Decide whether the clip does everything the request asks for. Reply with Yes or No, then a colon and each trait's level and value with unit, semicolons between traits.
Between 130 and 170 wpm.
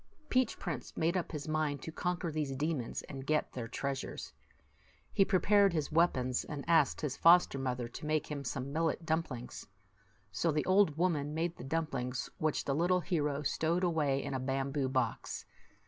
No: average, 180 wpm